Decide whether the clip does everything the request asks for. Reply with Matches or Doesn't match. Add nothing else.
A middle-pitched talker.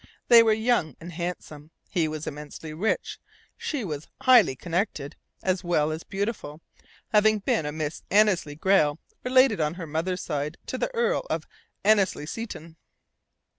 Matches